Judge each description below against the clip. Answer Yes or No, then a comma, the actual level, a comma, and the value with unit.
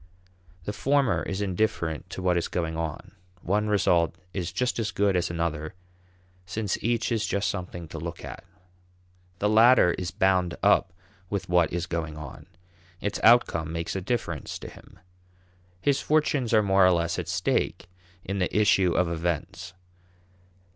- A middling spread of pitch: Yes, average, 3.7 semitones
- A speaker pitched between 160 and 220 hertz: No, very low, 90 Hz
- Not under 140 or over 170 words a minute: Yes, average, 160 wpm